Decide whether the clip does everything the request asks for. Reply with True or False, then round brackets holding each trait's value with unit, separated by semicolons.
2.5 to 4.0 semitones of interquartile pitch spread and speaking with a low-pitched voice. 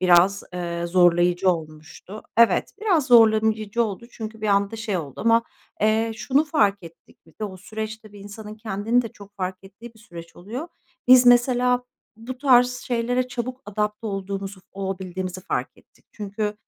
False (3.7 semitones; 215 Hz)